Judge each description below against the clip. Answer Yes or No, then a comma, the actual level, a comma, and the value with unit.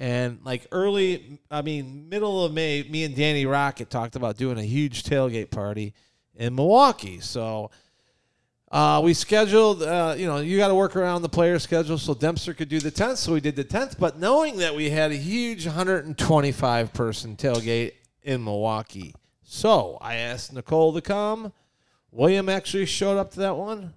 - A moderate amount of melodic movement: No, wide, 7.0 semitones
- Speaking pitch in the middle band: Yes, medium, 150 Hz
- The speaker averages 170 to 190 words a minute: Yes, average, 180 wpm